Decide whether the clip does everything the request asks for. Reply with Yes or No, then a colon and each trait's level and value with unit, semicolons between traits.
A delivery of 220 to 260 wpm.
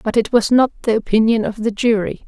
Yes: fast, 240 wpm